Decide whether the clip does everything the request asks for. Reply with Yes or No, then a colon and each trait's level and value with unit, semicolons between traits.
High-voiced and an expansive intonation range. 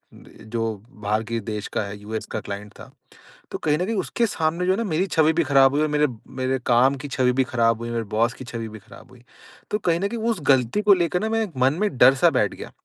No: low, 130 Hz; wide, 6.7 semitones